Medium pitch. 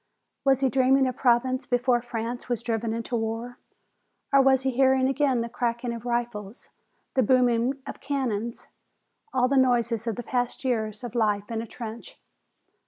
No: high, 240 Hz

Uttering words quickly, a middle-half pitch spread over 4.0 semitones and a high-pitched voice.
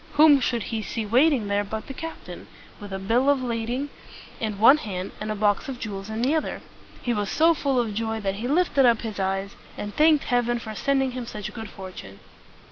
Yes: fast, 215 wpm; average, 4.5 semitones; high, 230 Hz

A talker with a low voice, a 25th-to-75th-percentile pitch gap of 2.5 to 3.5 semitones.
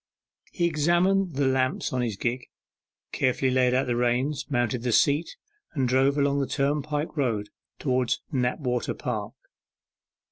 Yes: low, 130 Hz; average, 2.9 semitones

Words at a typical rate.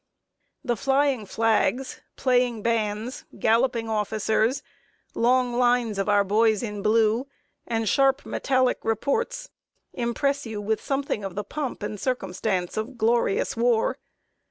No: slow, 125 wpm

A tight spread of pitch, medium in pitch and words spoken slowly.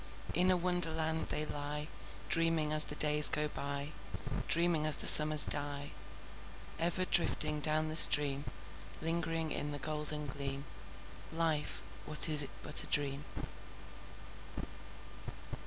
Yes: narrow, 1.7 semitones; medium, 150 Hz; slow, 125 wpm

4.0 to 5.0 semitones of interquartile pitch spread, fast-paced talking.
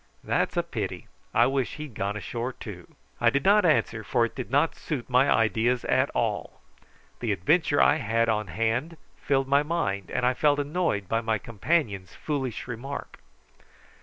No: average, 4.5 semitones; average, 170 wpm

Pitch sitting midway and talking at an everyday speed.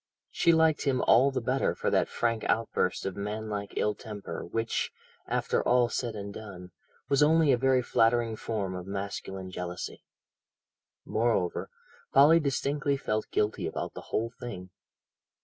No: low, 115 Hz; average, 150 wpm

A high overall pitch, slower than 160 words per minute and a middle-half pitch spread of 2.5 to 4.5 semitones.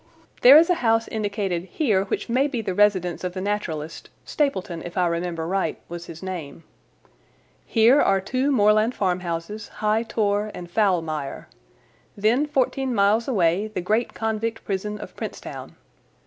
Yes: high, 205 Hz; average, 150 wpm; average, 4.1 semitones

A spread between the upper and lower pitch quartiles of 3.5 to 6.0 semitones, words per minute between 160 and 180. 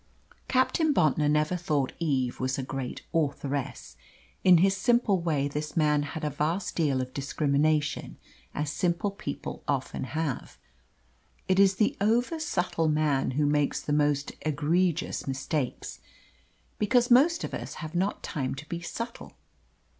No: average, 4.5 semitones; average, 140 wpm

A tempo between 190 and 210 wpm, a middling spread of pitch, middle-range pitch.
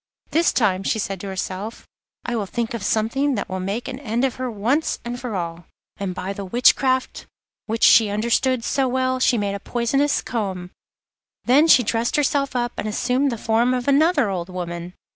No: average, 195 wpm; average, 4.5 semitones; high, 235 Hz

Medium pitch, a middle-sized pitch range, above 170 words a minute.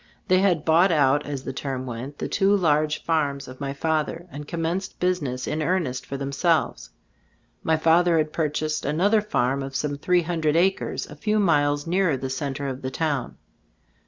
Yes: medium, 155 Hz; average, 3.6 semitones; average, 180 wpm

